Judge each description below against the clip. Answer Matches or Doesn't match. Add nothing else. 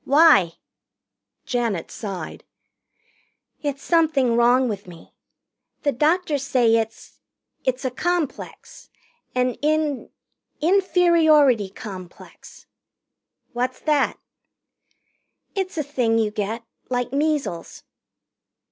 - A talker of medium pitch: Doesn't match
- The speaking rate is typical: Doesn't match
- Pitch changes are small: Doesn't match